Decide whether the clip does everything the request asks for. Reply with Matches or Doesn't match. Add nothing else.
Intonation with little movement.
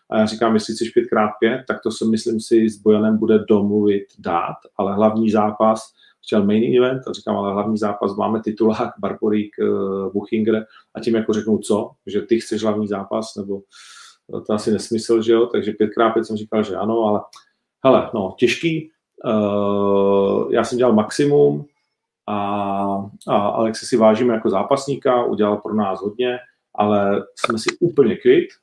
Matches